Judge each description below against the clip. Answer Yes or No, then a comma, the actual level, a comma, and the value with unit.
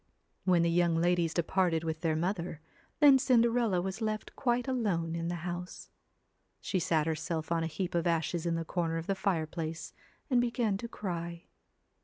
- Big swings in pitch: No, average, 3.3 semitones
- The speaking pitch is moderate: Yes, medium, 175 Hz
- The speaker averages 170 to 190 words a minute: Yes, average, 175 wpm